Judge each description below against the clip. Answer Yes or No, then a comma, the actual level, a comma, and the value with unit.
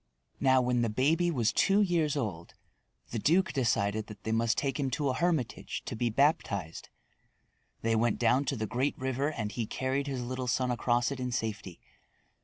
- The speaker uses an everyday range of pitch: Yes, average, 3.7 semitones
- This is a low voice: Yes, low, 125 Hz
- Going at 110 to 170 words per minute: No, average, 190 wpm